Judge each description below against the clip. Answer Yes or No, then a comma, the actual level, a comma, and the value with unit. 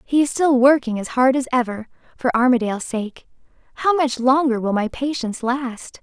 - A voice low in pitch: No, very high, 255 Hz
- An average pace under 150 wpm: No, average, 180 wpm